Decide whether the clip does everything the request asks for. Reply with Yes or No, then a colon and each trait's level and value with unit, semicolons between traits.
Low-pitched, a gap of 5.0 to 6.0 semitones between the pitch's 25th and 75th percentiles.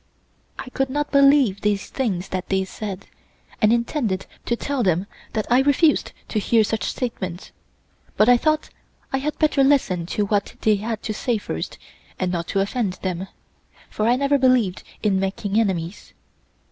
No: high, 215 Hz; average, 5.3 semitones